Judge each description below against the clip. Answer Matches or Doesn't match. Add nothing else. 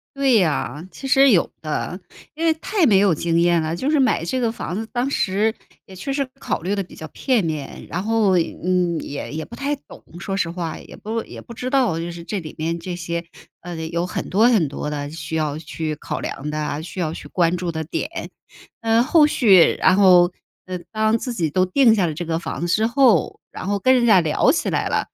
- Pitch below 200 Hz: Matches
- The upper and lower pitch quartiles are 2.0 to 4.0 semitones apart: Doesn't match